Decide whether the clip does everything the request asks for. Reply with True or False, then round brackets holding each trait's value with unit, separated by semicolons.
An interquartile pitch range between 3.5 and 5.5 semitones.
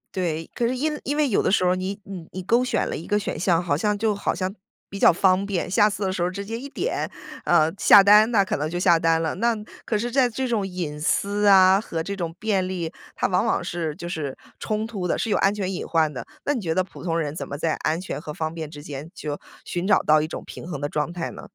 True (4.1 semitones)